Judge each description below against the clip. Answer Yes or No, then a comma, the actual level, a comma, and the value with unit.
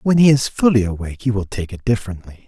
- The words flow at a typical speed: No, fast, 245 wpm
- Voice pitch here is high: No, low, 110 Hz